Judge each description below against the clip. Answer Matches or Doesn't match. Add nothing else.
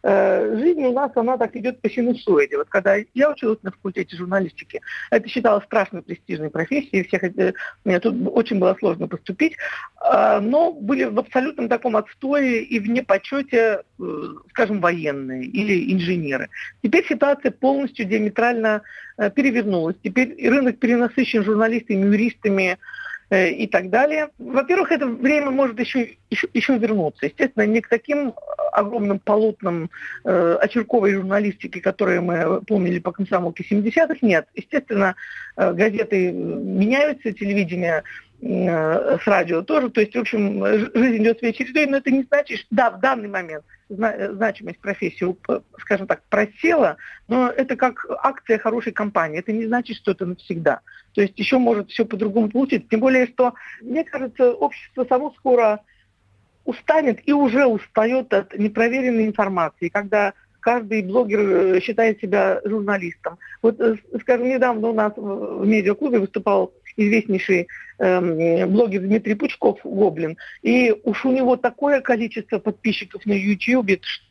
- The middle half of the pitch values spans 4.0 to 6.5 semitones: Matches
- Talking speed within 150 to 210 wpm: Doesn't match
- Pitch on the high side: Matches